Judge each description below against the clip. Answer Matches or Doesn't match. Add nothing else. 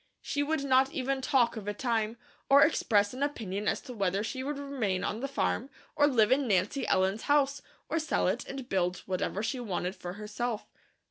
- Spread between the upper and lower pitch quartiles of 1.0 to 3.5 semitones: Doesn't match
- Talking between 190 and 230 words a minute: Matches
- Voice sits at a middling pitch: Doesn't match